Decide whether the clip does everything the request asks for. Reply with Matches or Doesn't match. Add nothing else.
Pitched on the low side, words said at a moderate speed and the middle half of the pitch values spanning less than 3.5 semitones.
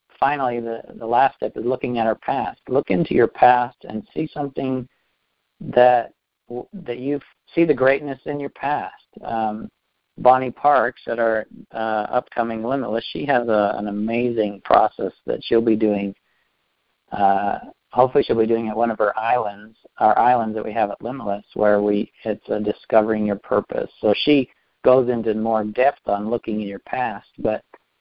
Matches